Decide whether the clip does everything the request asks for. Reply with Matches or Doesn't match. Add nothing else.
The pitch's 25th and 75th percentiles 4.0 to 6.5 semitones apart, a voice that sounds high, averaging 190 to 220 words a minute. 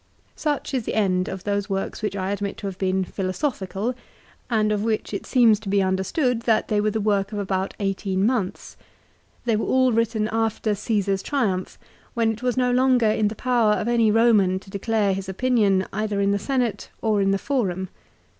Doesn't match